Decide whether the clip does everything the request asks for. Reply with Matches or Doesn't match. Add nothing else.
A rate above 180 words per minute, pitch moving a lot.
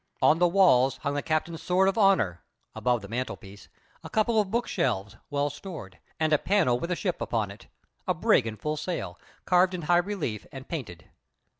Matches